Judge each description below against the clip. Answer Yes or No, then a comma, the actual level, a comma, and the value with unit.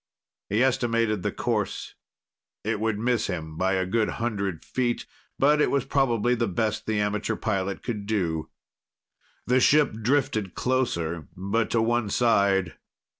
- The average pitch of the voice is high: No, low, 110 Hz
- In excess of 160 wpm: No, average, 145 wpm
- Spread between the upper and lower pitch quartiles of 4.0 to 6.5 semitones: No, average, 3.5 semitones